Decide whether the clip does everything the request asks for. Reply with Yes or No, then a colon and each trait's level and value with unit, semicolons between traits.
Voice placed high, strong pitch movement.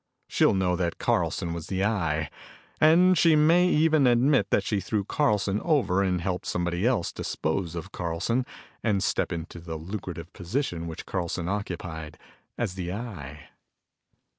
No: very low, 95 Hz; wide, 5.7 semitones